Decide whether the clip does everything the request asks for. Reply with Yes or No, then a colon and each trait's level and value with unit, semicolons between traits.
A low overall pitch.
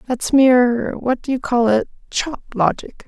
No: high, 245 Hz